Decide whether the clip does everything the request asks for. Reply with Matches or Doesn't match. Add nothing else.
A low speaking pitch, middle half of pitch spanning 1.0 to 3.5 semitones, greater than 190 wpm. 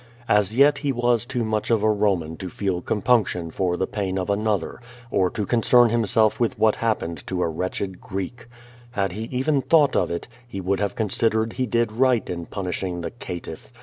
Doesn't match